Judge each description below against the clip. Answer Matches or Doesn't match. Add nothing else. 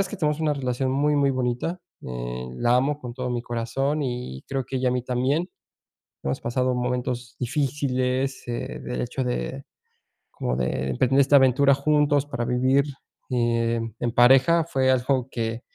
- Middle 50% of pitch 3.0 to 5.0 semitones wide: Doesn't match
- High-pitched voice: Doesn't match